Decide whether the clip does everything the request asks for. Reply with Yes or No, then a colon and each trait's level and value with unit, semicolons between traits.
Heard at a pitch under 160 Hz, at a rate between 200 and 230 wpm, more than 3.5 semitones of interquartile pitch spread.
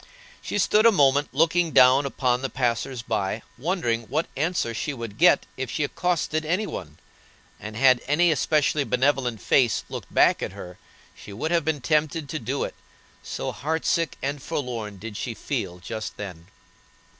No: low, 135 Hz; average, 170 wpm; average, 5.3 semitones